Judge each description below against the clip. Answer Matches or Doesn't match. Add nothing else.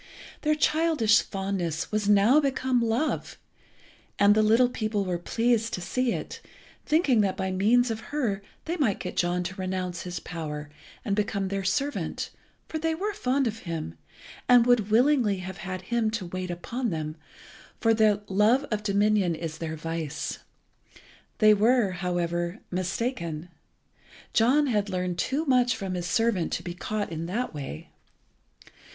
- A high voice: Matches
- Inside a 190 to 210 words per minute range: Doesn't match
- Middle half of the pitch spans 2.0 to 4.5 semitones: Doesn't match